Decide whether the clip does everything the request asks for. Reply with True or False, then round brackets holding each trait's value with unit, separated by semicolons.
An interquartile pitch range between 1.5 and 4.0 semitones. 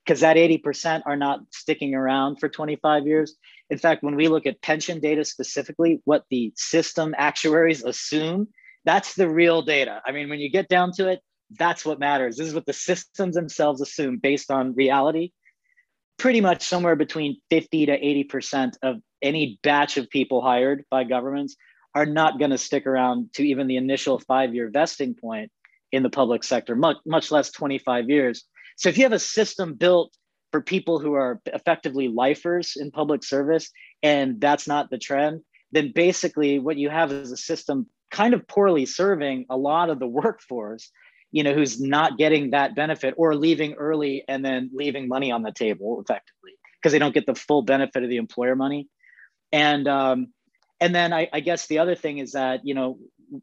True (3.2 semitones)